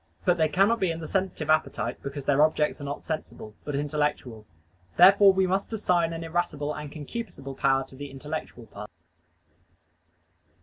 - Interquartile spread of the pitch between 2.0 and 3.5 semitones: No, average, 3.9 semitones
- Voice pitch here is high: No, medium, 155 Hz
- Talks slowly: No, average, 165 wpm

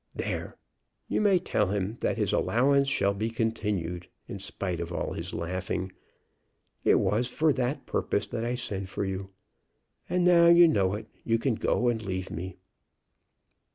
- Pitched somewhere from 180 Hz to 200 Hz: No, low, 105 Hz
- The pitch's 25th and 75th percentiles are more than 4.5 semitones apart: Yes, average, 5.0 semitones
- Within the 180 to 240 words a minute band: No, average, 165 wpm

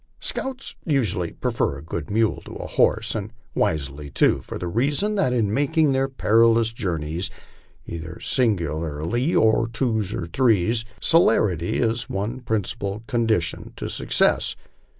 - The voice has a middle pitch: No, low, 110 Hz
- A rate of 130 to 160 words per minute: Yes, average, 145 wpm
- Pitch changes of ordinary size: No, wide, 6.0 semitones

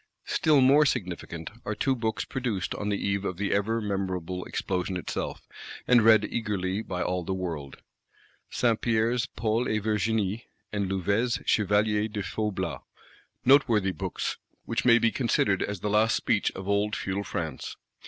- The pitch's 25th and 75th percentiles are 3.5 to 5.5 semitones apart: No, average, 3.0 semitones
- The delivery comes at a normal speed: Yes, average, 155 wpm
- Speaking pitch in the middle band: No, low, 105 Hz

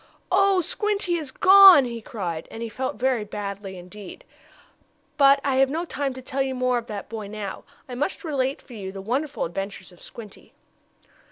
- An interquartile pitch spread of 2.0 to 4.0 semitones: No, wide, 5.6 semitones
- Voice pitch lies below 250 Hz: No, very high, 255 Hz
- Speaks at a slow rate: No, average, 185 wpm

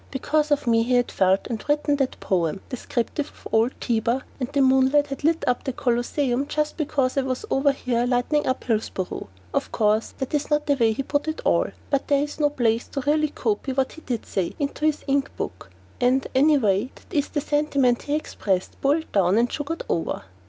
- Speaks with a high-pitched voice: Yes, very high, 265 Hz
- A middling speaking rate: No, fast, 210 wpm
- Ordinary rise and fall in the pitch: Yes, average, 3.7 semitones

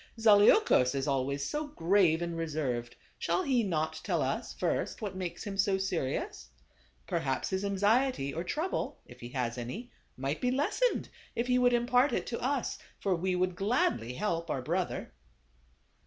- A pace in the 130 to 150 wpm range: No, average, 165 wpm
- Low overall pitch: No, medium, 185 Hz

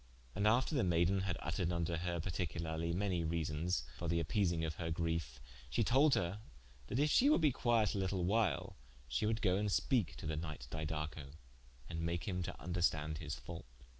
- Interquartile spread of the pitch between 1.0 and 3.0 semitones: No, average, 3.7 semitones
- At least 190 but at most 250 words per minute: Yes, average, 195 wpm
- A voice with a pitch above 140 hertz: No, very low, 85 Hz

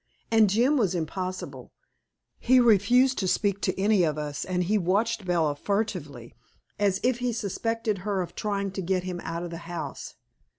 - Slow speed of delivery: No, average, 175 wpm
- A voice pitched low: No, high, 195 Hz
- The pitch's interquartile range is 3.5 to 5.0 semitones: Yes, average, 3.8 semitones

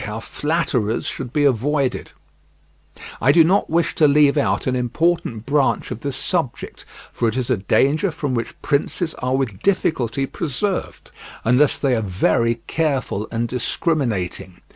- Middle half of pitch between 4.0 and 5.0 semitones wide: Yes, average, 4.6 semitones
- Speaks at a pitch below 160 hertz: Yes, low, 135 Hz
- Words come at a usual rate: Yes, average, 150 wpm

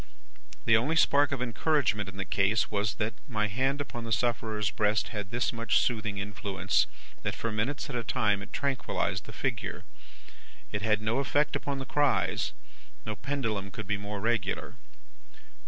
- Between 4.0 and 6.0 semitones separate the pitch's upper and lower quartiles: No, average, 3.5 semitones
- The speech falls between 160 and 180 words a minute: Yes, average, 170 wpm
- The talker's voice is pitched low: Yes, low, 110 Hz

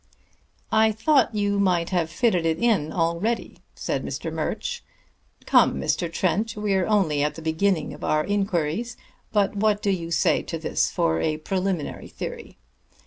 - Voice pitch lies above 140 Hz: Yes, high, 190 Hz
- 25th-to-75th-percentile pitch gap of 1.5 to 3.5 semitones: No, average, 4.2 semitones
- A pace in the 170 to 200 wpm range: No, average, 155 wpm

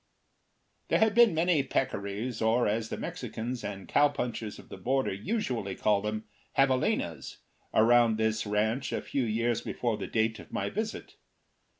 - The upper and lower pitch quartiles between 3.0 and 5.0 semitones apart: Yes, average, 3.7 semitones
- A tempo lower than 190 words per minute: Yes, average, 155 wpm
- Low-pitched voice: Yes, low, 115 Hz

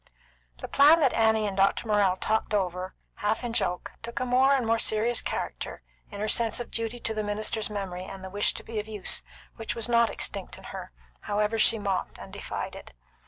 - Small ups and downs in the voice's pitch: Yes, narrow, 2.2 semitones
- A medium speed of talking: No, fast, 210 wpm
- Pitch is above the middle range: Yes, high, 215 Hz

